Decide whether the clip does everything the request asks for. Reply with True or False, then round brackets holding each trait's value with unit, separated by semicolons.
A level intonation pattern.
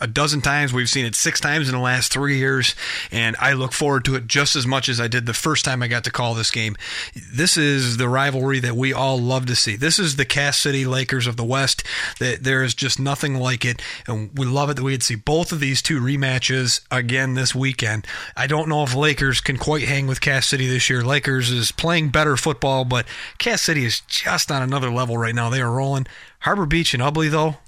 True (2.3 semitones)